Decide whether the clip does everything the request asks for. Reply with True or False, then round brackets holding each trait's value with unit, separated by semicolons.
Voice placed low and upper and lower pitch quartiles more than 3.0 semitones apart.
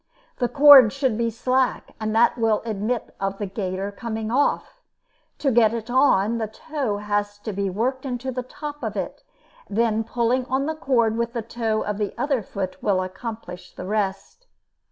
False (225 Hz; 3.7 semitones)